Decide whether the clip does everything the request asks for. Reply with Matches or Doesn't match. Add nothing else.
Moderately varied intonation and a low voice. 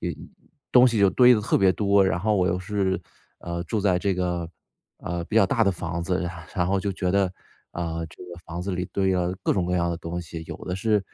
Doesn't match